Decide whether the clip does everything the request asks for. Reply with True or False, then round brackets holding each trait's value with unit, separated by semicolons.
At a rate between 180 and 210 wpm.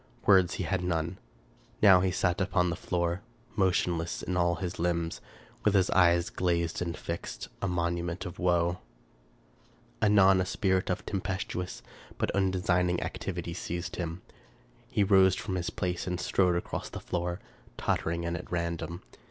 False (150 wpm)